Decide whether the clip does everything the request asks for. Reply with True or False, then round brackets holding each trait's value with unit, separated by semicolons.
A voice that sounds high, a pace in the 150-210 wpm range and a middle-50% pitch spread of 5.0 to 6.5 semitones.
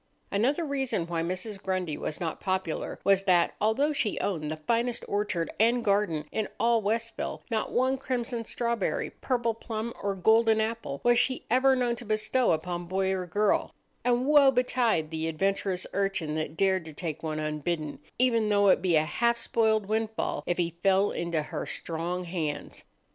True (200 Hz; 175 wpm; 5.3 semitones)